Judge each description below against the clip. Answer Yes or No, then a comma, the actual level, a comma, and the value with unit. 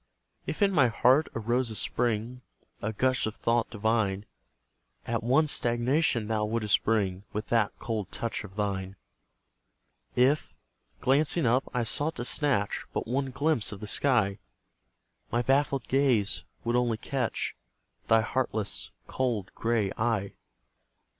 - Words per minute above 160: No, slow, 135 wpm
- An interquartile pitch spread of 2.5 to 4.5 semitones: Yes, average, 3.4 semitones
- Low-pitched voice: Yes, low, 115 Hz